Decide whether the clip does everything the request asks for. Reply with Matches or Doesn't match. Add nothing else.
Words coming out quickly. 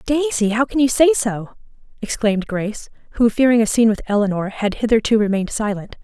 Doesn't match